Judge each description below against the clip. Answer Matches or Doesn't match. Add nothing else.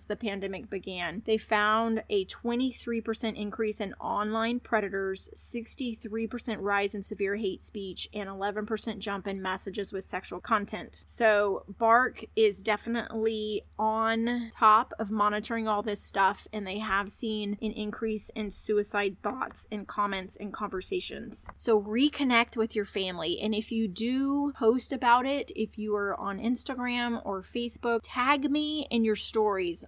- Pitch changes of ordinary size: Doesn't match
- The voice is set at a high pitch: Matches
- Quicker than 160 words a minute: Doesn't match